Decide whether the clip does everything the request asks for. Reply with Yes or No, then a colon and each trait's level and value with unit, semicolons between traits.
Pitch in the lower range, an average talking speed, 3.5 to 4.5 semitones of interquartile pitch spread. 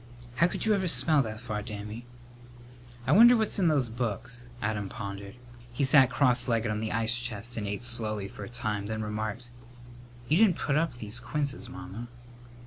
Yes: low, 120 Hz; average, 185 wpm; average, 3.9 semitones